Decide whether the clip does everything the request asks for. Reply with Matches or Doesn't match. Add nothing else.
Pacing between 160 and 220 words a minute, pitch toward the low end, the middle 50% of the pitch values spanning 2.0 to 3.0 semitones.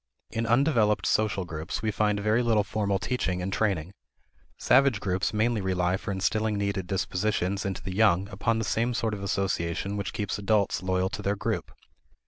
Matches